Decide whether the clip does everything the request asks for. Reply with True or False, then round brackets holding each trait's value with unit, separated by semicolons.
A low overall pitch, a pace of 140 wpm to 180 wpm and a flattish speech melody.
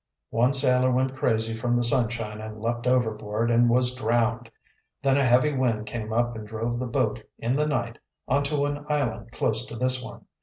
False (120 Hz; 190 wpm; 2.3 semitones)